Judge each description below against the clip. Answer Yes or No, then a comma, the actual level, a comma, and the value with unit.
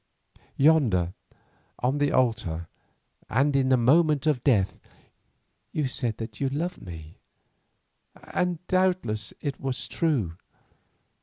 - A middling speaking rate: No, slow, 110 wpm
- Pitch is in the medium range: No, low, 130 Hz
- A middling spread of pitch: No, wide, 6.0 semitones